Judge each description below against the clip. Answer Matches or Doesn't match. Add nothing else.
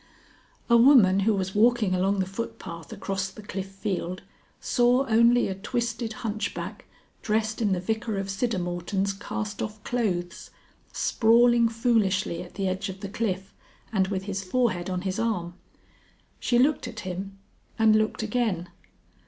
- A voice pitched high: Matches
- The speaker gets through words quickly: Doesn't match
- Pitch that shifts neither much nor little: Matches